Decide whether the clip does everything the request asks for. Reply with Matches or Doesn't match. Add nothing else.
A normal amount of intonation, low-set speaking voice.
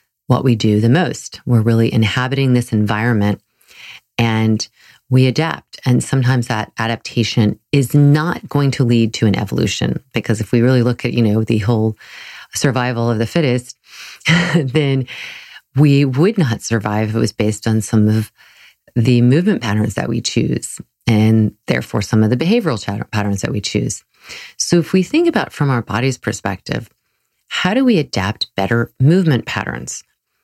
Matches